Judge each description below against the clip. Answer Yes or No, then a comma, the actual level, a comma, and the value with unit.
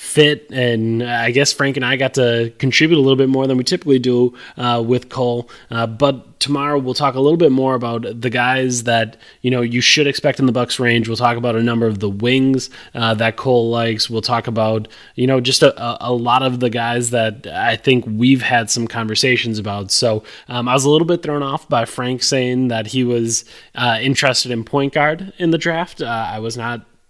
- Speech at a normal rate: No, fast, 225 wpm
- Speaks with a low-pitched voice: Yes, low, 125 Hz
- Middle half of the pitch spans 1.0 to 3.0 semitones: Yes, narrow, 2.4 semitones